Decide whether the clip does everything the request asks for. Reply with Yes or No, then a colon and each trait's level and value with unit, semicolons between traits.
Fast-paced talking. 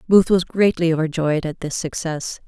No: average, 170 wpm